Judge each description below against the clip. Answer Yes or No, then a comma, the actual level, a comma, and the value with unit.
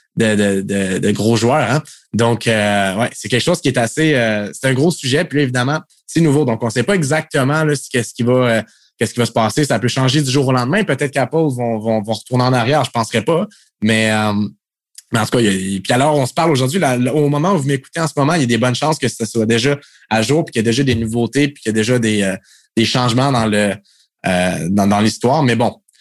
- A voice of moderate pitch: No, low, 125 Hz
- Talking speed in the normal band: No, fast, 280 wpm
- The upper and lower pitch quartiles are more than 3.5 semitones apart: Yes, average, 4.5 semitones